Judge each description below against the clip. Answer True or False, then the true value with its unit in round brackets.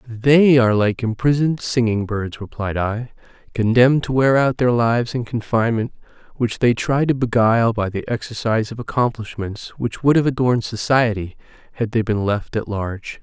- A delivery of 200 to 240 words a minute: False (170 wpm)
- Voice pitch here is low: True (115 Hz)